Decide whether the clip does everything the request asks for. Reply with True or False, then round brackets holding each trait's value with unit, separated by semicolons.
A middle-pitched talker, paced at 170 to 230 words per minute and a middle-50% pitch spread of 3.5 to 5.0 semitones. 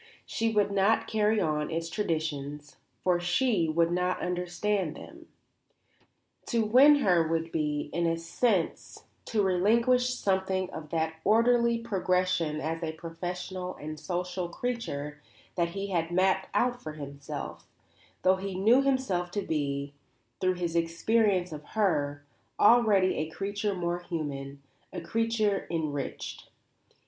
False (180 Hz; 135 wpm; 4.4 semitones)